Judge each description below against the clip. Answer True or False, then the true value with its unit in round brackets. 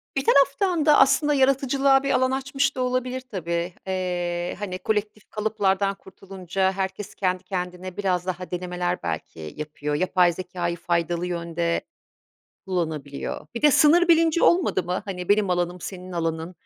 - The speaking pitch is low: False (185 Hz)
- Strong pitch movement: True (6.4 semitones)